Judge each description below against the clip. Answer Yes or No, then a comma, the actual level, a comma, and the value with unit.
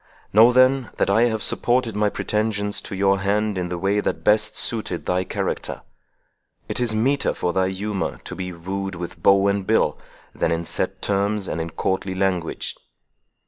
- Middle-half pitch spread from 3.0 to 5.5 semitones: No, narrow, 2.5 semitones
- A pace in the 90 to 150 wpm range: No, average, 180 wpm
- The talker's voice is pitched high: No, low, 100 Hz